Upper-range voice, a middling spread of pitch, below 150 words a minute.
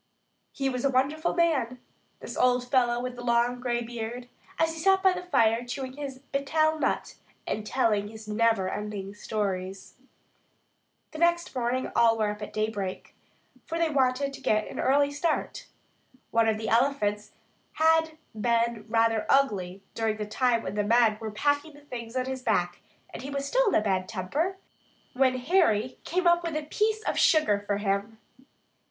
No: high, 245 Hz; average, 5.0 semitones; average, 175 wpm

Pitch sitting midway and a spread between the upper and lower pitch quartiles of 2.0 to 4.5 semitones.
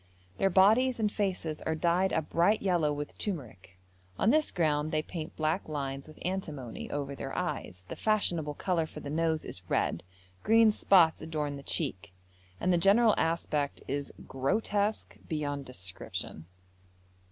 No: medium, 160 Hz; average, 5.1 semitones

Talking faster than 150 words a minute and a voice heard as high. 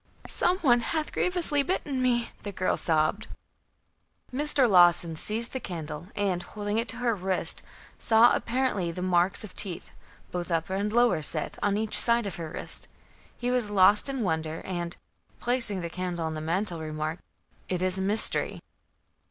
Yes: average, 170 wpm; high, 195 Hz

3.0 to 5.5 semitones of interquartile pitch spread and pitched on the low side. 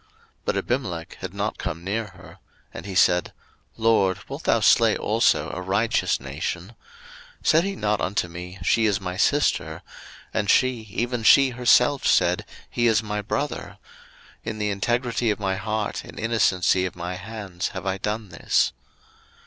Yes: average, 3.7 semitones; low, 105 Hz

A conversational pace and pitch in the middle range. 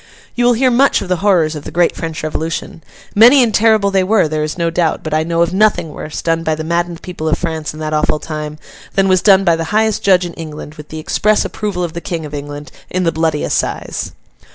No: fast, 250 wpm; medium, 170 Hz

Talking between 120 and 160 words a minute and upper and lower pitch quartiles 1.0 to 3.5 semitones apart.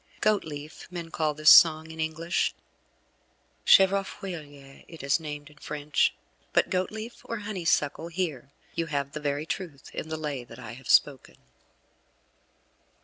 Yes: average, 140 wpm; average, 3.1 semitones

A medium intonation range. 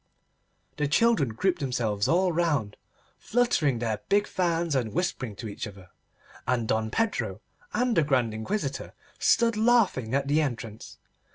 No: wide, 8.5 semitones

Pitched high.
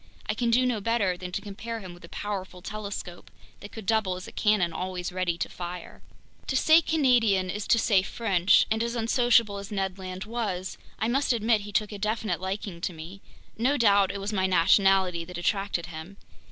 Yes: high, 200 Hz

